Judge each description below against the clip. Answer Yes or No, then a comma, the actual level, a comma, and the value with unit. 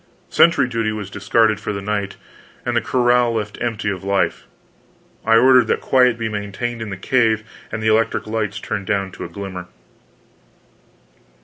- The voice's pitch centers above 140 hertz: No, low, 110 Hz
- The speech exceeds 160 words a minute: Yes, average, 170 wpm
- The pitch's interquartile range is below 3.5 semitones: Yes, average, 2.7 semitones